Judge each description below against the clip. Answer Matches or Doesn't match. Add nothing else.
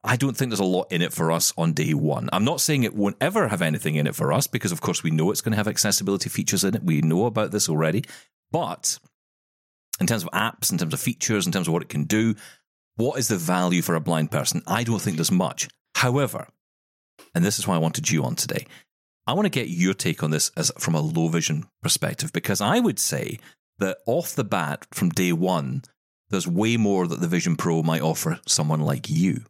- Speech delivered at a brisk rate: Matches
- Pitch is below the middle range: Matches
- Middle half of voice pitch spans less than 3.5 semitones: Doesn't match